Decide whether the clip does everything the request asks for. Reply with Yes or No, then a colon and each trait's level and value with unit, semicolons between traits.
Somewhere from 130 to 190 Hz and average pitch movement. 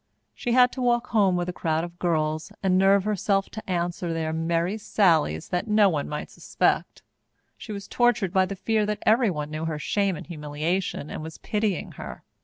Yes: medium, 185 Hz; average, 4.5 semitones